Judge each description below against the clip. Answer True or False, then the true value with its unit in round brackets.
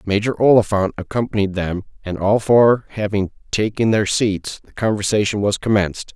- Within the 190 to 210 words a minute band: False (145 wpm)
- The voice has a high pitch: False (105 Hz)